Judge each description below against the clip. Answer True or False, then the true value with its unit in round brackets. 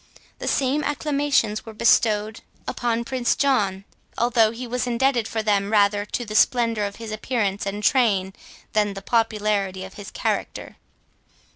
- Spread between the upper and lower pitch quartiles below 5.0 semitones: True (3.0 semitones)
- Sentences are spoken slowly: False (155 wpm)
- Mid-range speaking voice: False (220 Hz)